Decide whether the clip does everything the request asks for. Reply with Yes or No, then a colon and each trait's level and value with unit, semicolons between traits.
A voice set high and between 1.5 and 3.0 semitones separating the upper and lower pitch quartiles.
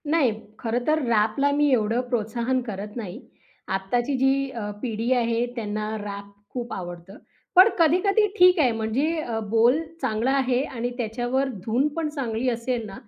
No: high, 240 Hz; average, 3.8 semitones